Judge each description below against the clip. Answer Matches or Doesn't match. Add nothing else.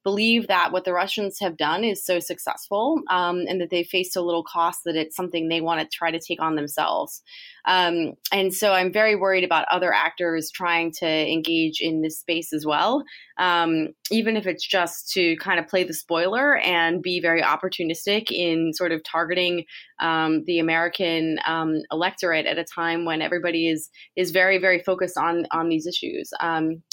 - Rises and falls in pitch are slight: Matches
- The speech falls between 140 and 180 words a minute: Doesn't match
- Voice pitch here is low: Doesn't match